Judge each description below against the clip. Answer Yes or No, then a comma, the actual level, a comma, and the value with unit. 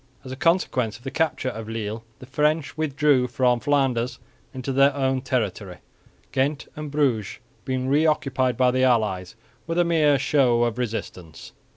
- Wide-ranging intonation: No, average, 3.5 semitones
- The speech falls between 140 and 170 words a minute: Yes, average, 165 wpm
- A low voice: Yes, low, 130 Hz